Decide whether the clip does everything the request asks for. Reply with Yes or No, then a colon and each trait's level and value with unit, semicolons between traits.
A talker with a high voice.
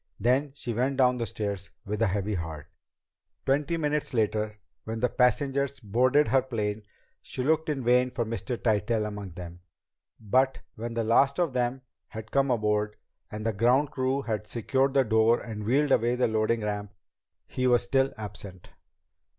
No: low, 120 Hz